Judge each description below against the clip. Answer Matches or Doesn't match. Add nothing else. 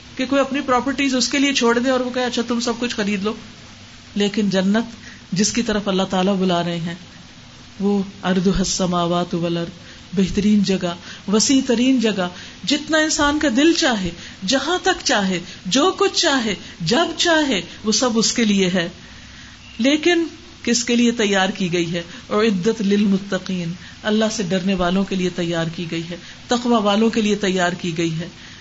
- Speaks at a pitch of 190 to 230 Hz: Matches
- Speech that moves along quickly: Doesn't match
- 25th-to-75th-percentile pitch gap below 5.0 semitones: Doesn't match